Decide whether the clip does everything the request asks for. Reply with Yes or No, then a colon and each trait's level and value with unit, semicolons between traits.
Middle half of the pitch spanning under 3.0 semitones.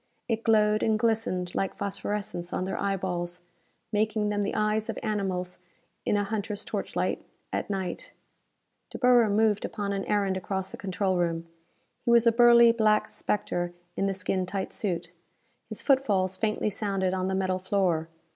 Yes: narrow, 2.4 semitones